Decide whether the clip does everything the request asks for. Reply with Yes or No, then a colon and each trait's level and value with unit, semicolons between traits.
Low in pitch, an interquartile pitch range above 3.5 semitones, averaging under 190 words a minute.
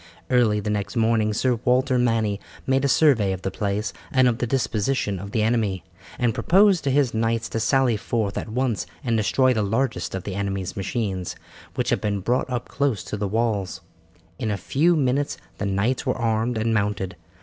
No: low, 115 Hz; average, 3.9 semitones; average, 195 wpm